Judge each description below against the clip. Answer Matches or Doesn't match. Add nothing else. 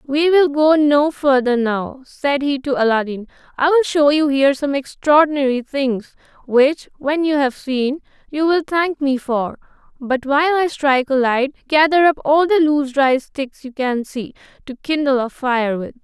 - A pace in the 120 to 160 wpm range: Doesn't match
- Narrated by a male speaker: Doesn't match